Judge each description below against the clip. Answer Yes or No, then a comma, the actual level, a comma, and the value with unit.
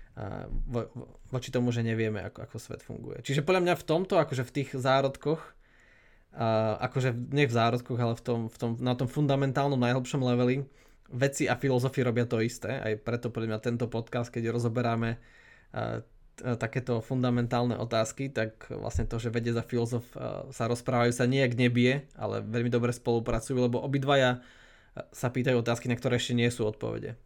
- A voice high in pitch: No, low, 120 Hz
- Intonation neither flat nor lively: No, narrow, 2.0 semitones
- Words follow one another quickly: Yes, fast, 170 wpm